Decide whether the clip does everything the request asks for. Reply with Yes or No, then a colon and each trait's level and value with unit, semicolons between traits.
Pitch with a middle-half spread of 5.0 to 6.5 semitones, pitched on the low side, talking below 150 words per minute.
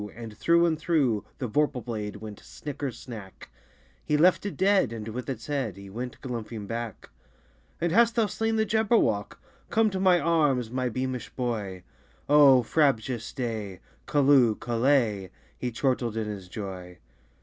No: wide, 5.5 semitones; low, 125 Hz; average, 155 wpm